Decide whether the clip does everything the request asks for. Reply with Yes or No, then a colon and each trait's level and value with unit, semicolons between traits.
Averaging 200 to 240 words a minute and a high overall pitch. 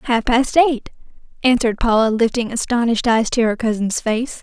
No: average, 165 wpm; high, 235 Hz